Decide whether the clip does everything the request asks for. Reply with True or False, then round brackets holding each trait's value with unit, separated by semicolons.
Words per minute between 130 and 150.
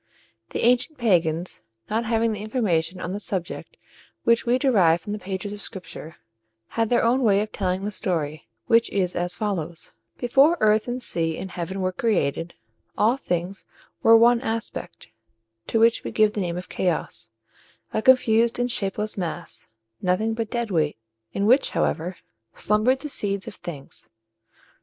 False (165 wpm)